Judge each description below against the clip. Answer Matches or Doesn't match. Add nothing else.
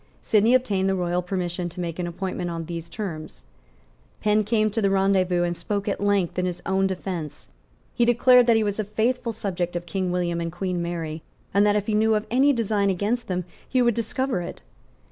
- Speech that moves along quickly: Matches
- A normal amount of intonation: Matches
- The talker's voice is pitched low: Doesn't match